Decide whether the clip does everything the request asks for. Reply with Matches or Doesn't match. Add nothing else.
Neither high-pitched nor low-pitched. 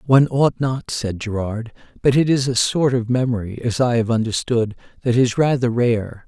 Doesn't match